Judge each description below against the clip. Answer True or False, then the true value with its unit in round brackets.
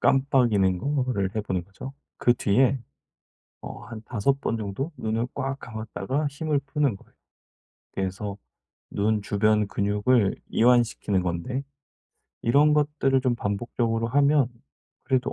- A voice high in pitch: False (115 Hz)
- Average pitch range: True (4.8 semitones)